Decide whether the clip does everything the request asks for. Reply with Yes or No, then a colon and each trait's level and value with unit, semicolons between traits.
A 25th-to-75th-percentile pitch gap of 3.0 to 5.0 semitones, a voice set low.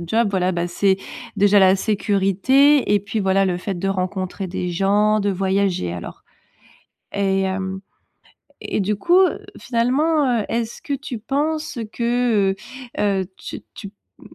No: average, 3.7 semitones; high, 200 Hz